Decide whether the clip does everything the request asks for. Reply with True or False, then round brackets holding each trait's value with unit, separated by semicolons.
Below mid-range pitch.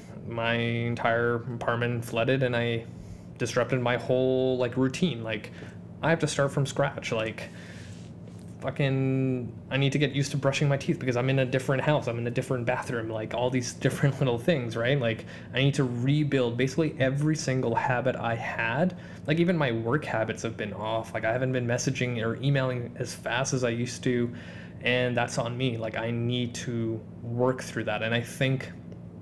True (125 Hz)